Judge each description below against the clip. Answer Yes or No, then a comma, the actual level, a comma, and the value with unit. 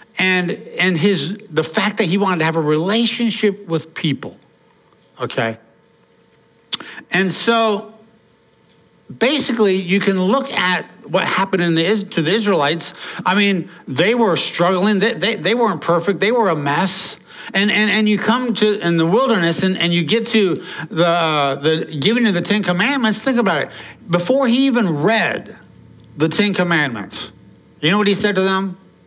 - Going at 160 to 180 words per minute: Yes, average, 165 wpm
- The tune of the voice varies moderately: Yes, average, 4.5 semitones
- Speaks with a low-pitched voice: No, high, 190 Hz